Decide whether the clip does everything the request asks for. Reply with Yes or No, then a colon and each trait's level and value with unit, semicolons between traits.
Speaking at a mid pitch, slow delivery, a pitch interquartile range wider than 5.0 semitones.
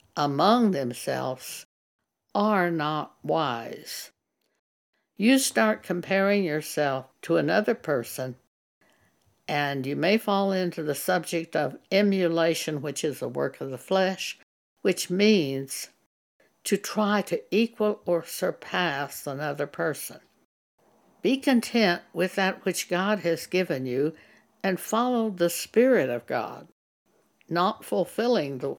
Yes: medium, 180 Hz; slow, 115 wpm; wide, 5.4 semitones